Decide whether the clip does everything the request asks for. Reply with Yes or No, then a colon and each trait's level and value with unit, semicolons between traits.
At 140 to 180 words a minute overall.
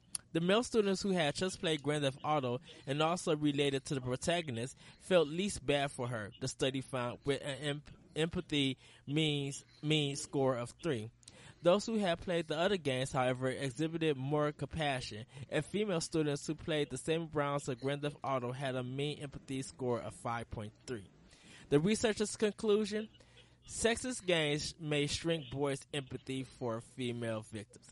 Yes: average, 165 wpm